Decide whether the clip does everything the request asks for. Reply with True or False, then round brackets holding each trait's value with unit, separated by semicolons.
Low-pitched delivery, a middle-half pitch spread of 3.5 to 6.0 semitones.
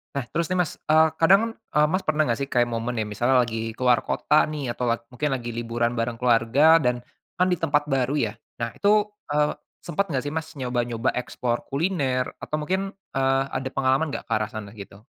True (130 Hz; 4.5 semitones)